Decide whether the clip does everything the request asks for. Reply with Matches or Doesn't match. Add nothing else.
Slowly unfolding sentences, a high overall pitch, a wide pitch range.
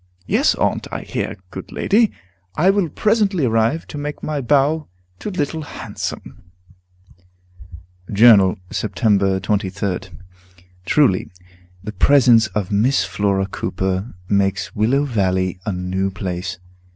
Doesn't match